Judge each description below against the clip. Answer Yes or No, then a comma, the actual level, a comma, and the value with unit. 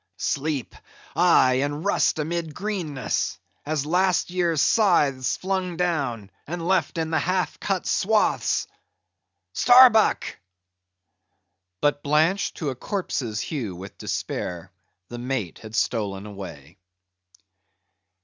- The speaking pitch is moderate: Yes, medium, 155 Hz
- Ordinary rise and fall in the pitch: No, wide, 6.4 semitones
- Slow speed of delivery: Yes, slow, 105 wpm